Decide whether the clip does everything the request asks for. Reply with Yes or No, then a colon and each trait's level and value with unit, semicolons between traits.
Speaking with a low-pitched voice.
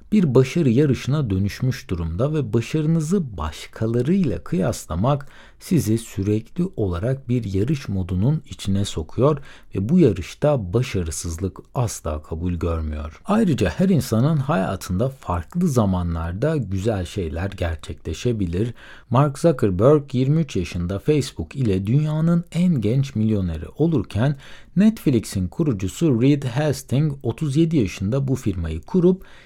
Yes: low, 120 Hz